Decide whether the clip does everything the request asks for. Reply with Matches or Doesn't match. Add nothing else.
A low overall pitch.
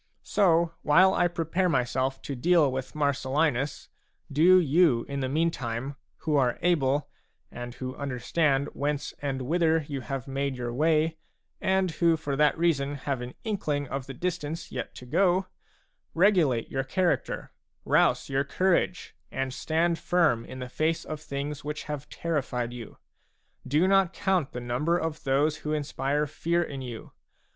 Doesn't match